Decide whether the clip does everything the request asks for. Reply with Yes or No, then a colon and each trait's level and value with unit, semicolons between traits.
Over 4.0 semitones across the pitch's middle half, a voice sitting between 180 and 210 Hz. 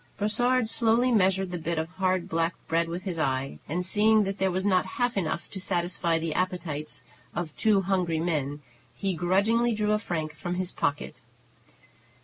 No: average, 3.6 semitones; medium, 185 Hz